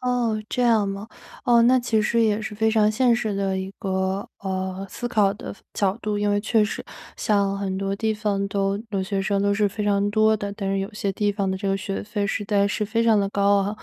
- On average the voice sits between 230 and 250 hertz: No, high, 205 Hz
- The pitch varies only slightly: Yes, narrow, 1.8 semitones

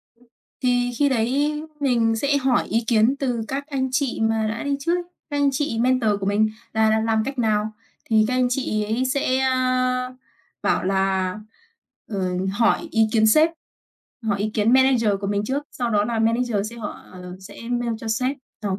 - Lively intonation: No, average, 3.3 semitones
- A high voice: Yes, high, 235 Hz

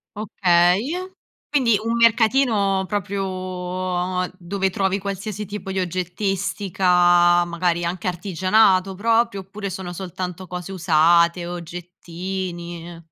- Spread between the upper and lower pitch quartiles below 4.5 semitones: Yes, narrow, 2.5 semitones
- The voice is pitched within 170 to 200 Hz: Yes, medium, 185 Hz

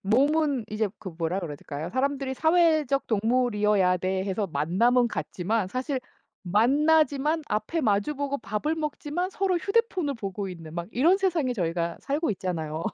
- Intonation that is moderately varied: No, wide, 8.1 semitones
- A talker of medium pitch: No, high, 235 Hz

